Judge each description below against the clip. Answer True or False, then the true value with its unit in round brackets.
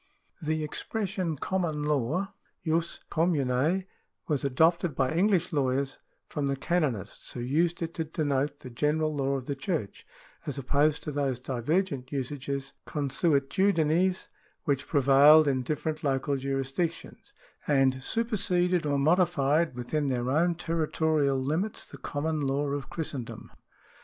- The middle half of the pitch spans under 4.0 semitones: True (3.4 semitones)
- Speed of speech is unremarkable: False (130 wpm)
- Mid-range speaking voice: True (150 Hz)